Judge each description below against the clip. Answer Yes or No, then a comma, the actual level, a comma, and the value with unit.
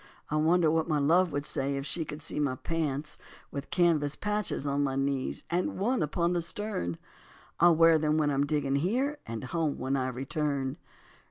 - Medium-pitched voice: Yes, medium, 150 Hz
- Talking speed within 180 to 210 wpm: Yes, average, 190 wpm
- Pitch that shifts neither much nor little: Yes, average, 3.4 semitones